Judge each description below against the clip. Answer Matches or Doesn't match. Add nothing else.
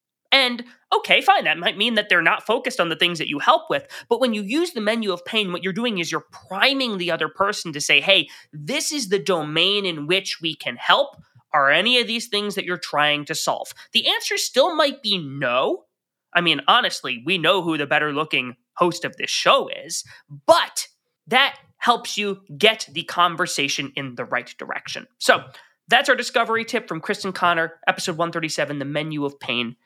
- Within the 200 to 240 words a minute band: Matches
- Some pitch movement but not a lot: Doesn't match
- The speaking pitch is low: Doesn't match